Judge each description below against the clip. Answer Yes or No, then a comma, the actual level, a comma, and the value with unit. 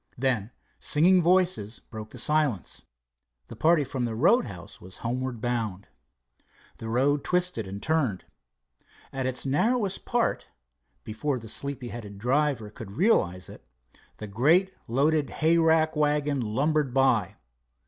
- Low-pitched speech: Yes, low, 130 Hz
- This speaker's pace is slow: Yes, slow, 130 wpm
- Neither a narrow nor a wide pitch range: No, wide, 5.9 semitones